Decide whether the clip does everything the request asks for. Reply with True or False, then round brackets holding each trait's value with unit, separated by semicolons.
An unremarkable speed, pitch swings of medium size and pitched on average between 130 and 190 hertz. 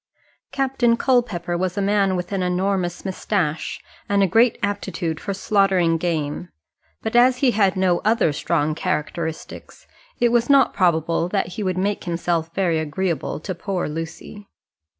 True (150 wpm; 3.4 semitones; 185 Hz)